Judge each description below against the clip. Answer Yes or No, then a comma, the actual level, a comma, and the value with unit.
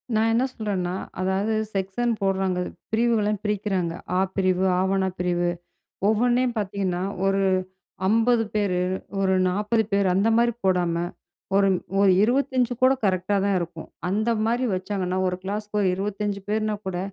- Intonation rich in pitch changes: No, average, 2.8 semitones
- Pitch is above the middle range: Yes, high, 200 Hz